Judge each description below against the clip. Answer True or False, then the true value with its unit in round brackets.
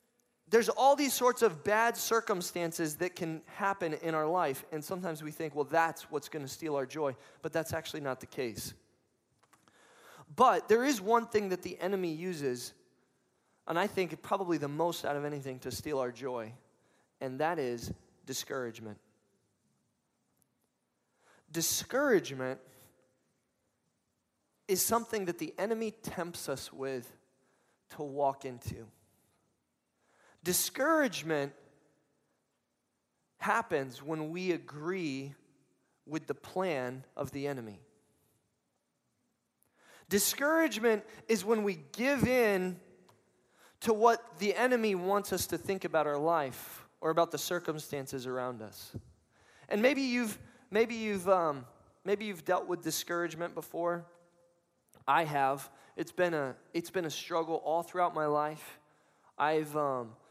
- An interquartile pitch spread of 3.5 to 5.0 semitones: False (5.6 semitones)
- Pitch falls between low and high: True (165 Hz)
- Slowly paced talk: True (130 wpm)